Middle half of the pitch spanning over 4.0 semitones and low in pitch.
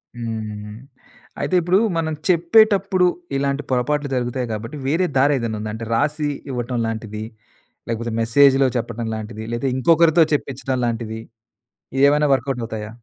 Yes: average, 4.5 semitones; low, 130 Hz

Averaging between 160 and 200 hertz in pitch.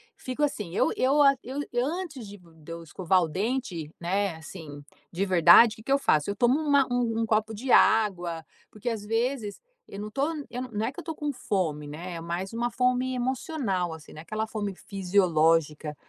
No: high, 210 Hz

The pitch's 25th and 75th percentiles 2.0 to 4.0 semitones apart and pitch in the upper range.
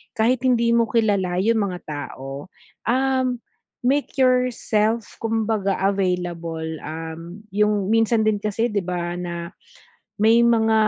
No: average, 4.5 semitones; high, 210 Hz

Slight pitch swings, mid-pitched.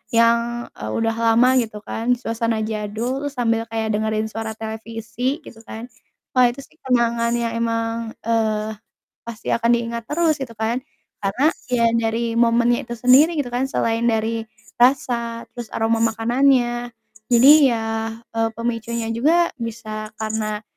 No: narrow, 1.4 semitones; high, 230 Hz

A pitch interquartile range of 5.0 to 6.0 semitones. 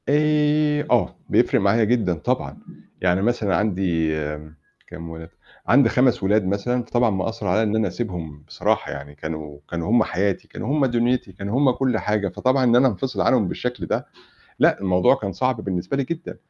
Yes: wide, 5.5 semitones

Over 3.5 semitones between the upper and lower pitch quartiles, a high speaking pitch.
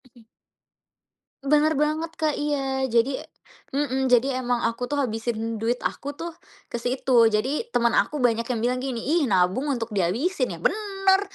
Yes: average, 4.2 semitones; very high, 260 Hz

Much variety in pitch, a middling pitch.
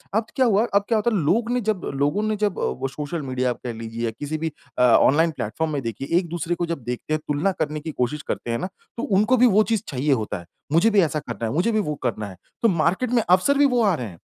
Yes: wide, 7.8 semitones; medium, 160 Hz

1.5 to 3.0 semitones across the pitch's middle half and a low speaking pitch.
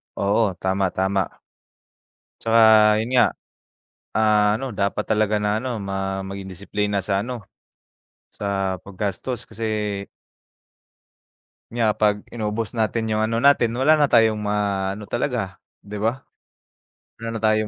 Yes: narrow, 2.4 semitones; low, 105 Hz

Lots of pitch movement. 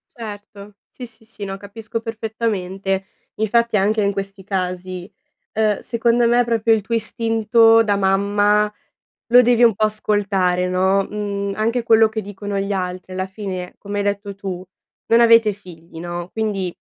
No: narrow, 2.6 semitones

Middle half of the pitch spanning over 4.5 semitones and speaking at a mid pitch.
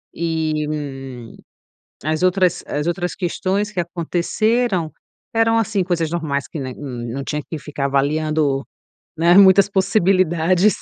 No: average, 4.1 semitones; medium, 170 Hz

